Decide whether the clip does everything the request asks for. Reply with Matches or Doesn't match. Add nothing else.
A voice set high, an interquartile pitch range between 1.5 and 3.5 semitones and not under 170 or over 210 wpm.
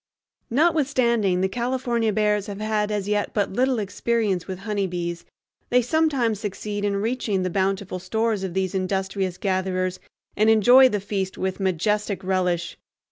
Doesn't match